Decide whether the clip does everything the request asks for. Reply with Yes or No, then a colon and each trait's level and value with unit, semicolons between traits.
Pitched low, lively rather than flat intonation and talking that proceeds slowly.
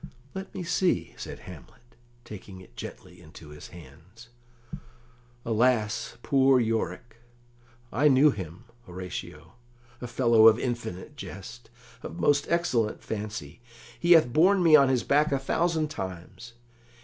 Yes: low, 115 Hz; wide, 7.5 semitones; slow, 130 wpm